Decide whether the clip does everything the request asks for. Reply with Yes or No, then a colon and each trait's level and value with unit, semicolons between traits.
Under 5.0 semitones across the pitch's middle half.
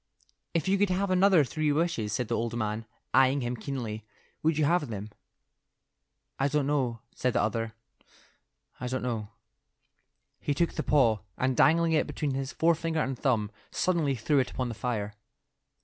No: wide, 5.5 semitones